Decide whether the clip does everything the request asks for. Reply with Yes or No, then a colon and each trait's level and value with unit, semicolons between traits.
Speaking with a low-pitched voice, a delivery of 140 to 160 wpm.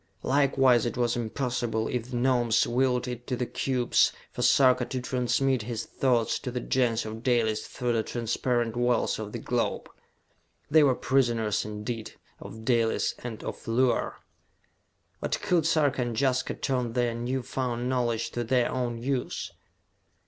Yes: low, 120 Hz; average, 155 wpm